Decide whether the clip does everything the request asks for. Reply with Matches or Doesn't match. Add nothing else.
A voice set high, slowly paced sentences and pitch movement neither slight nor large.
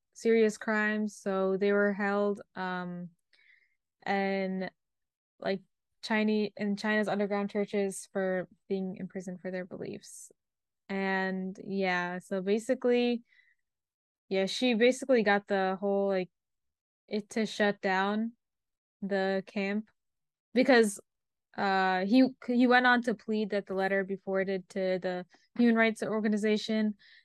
Doesn't match